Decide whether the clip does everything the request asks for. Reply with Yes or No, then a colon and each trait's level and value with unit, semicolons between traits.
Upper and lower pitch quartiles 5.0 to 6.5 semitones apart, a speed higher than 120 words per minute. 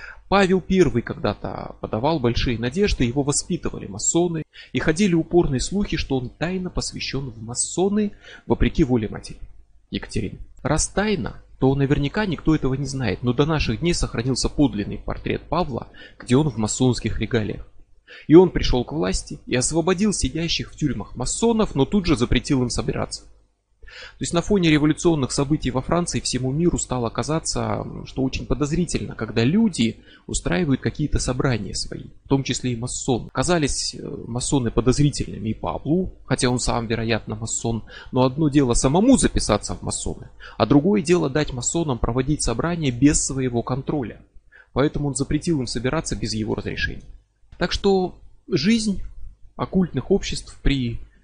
Yes: average, 5.3 semitones; average, 150 wpm